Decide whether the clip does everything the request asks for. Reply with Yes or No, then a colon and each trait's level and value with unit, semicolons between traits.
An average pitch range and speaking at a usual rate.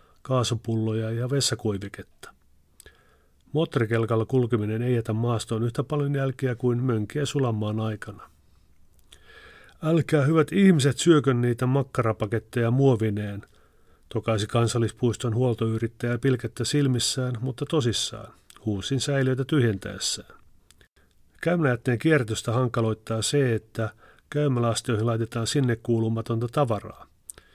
No: average, 3.4 semitones; slow, 90 wpm